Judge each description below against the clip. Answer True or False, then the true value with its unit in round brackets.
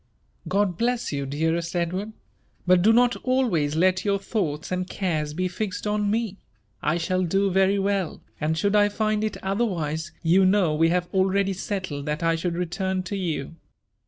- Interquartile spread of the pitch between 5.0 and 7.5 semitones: False (3.5 semitones)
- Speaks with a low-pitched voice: False (185 Hz)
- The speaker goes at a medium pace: True (180 wpm)